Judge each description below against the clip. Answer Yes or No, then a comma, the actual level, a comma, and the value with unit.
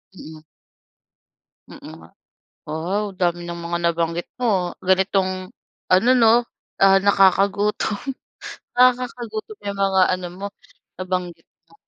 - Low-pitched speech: No, high, 190 Hz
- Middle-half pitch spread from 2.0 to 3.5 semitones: Yes, average, 2.9 semitones